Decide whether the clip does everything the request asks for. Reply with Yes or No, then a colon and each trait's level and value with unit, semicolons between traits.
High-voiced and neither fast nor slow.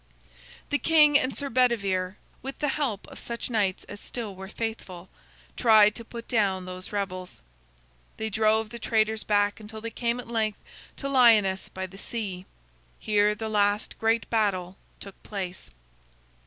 Yes: high, 215 Hz; average, 155 wpm